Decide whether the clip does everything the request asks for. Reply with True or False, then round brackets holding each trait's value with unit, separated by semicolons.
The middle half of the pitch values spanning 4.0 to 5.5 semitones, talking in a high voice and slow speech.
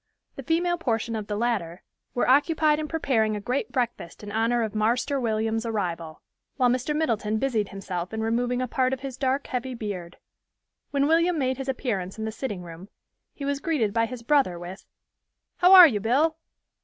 False (4.5 semitones; 240 Hz; 190 wpm)